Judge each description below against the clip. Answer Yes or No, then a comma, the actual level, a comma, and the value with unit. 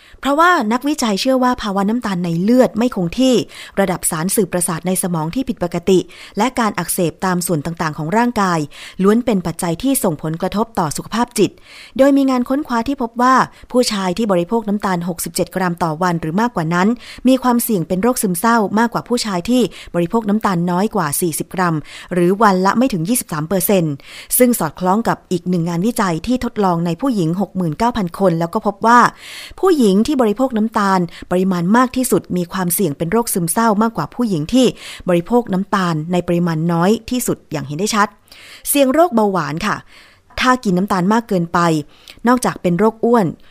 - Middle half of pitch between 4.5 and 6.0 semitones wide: Yes, average, 5.0 semitones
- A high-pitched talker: Yes, high, 195 Hz